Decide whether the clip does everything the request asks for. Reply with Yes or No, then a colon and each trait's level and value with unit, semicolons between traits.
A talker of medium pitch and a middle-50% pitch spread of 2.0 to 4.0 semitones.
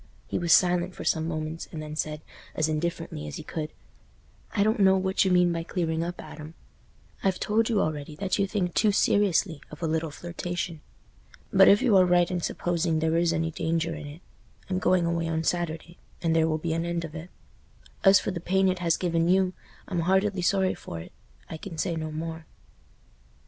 Yes: medium, 170 Hz; narrow, 2.5 semitones